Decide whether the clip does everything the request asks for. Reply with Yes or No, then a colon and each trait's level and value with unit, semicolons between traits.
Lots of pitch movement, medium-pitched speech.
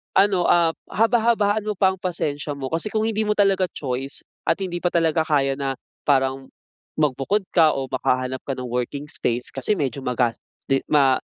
Yes: wide, 6.3 semitones; medium, 150 Hz